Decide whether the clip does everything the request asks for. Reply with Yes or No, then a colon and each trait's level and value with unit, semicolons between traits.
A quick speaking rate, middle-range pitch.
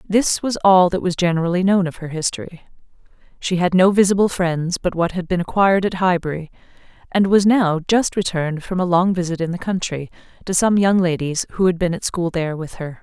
Yes: fast, 210 wpm; medium, 180 Hz